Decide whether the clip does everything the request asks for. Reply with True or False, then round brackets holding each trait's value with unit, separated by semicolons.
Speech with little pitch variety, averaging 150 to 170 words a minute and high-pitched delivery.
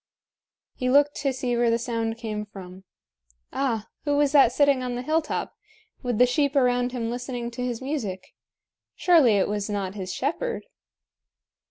False (3.7 semitones; 165 wpm; 245 Hz)